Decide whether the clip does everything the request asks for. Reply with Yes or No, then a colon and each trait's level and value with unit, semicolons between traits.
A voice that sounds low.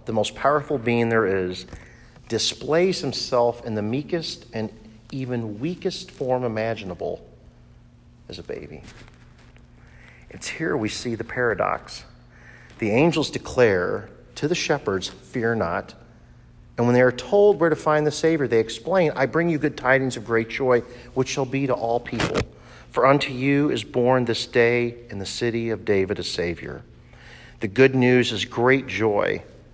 Yes: low, 120 Hz